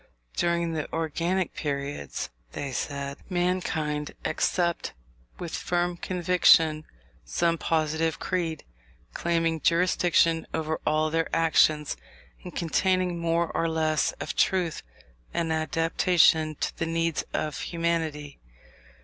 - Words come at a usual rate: No, slow, 105 wpm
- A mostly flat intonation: Yes, narrow, 1.7 semitones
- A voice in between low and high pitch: Yes, medium, 165 Hz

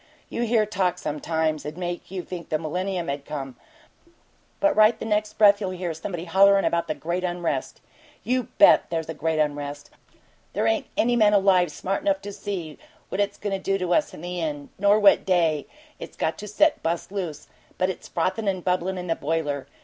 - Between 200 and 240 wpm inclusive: Yes, fast, 205 wpm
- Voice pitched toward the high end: No, medium, 180 Hz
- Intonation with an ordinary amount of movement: Yes, average, 4.0 semitones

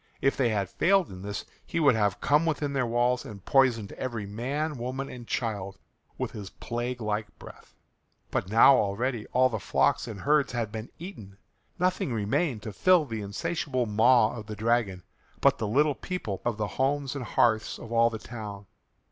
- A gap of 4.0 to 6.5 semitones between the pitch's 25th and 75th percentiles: Yes, average, 4.3 semitones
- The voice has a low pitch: Yes, low, 120 Hz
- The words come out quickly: No, average, 185 wpm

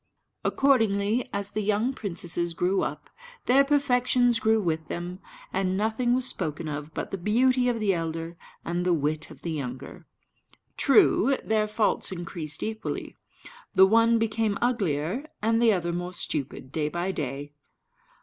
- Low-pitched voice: No, high, 195 Hz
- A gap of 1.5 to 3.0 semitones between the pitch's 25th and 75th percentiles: No, wide, 5.5 semitones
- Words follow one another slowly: No, average, 150 wpm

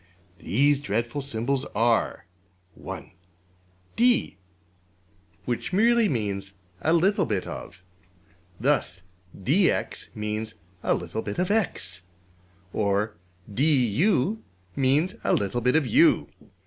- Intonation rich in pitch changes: Yes, wide, 8.3 semitones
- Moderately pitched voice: No, low, 125 Hz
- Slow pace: Yes, slow, 95 wpm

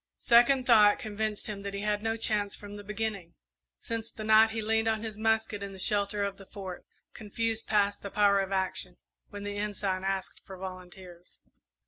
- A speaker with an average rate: Yes, average, 195 wpm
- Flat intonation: Yes, narrow, 1.9 semitones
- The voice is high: Yes, high, 205 Hz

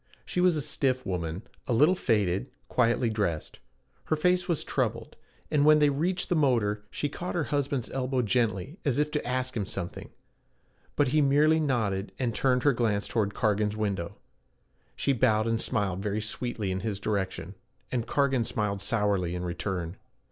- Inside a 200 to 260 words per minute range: No, average, 170 wpm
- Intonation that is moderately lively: No, wide, 5.7 semitones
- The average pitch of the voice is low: Yes, low, 115 Hz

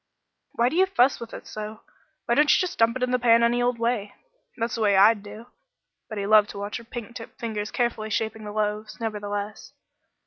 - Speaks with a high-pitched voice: Yes, high, 225 Hz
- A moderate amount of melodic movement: No, narrow, 2.2 semitones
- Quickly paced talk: Yes, fast, 220 wpm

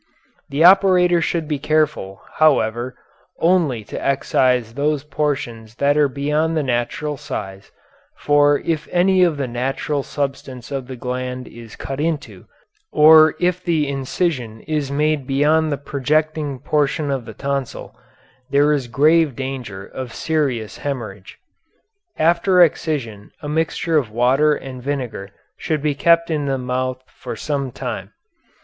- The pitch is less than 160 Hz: Yes, medium, 140 Hz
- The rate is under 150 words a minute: Yes, average, 140 wpm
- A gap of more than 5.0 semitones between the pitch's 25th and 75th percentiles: No, average, 3.4 semitones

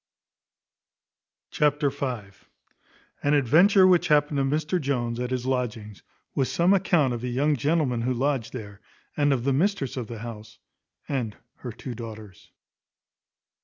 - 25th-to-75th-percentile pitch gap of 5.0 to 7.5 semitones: No, average, 4.0 semitones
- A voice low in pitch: Yes, low, 130 Hz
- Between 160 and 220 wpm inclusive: No, average, 145 wpm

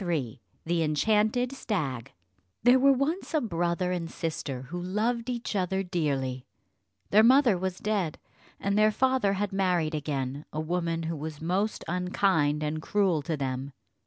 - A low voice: No, medium, 180 Hz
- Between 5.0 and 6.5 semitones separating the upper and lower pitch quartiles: Yes, wide, 5.4 semitones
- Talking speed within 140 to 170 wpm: Yes, average, 160 wpm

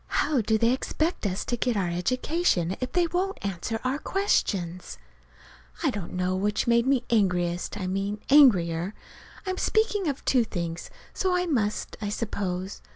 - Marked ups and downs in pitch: Yes, wide, 7.2 semitones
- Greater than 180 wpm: No, average, 160 wpm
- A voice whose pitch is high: Yes, high, 215 Hz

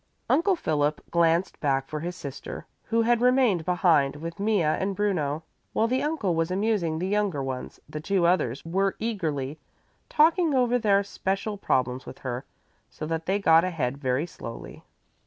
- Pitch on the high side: No, medium, 175 Hz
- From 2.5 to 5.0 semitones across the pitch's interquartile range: No, wide, 5.6 semitones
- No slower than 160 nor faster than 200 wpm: Yes, average, 165 wpm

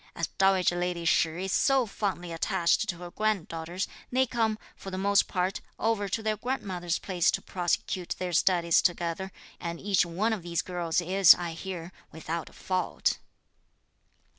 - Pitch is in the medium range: Yes, medium, 180 Hz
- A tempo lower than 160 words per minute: No, average, 165 wpm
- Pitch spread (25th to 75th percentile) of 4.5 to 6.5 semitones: No, average, 2.7 semitones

